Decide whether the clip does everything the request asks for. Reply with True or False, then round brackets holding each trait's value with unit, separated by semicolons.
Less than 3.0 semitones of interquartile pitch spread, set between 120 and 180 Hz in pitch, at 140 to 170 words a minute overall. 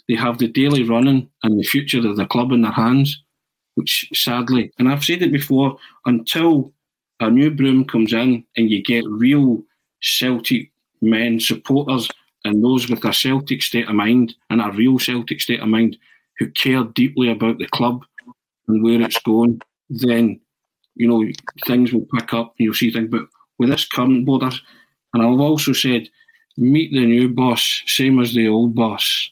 False (2.4 semitones; 125 Hz; 180 wpm)